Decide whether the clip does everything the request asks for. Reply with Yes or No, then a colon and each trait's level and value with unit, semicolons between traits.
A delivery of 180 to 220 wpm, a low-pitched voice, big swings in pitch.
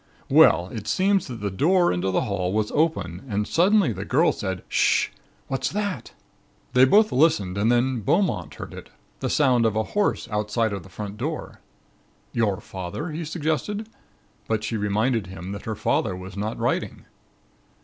No: average, 170 wpm; low, 110 Hz; wide, 7.7 semitones